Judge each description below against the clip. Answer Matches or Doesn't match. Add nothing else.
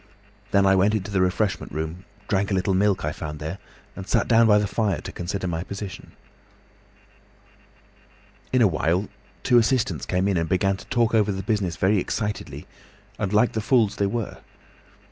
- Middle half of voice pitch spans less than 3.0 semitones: Matches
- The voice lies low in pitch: Matches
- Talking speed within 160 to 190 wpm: Matches